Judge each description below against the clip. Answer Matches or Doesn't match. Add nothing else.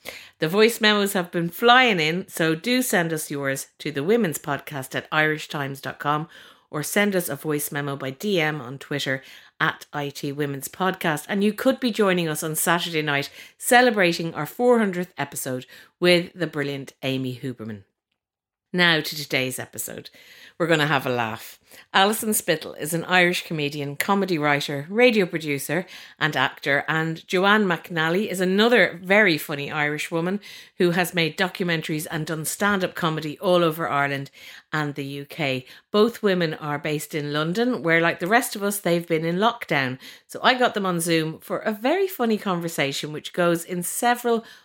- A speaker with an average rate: Matches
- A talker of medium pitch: Matches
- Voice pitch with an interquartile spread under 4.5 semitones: Doesn't match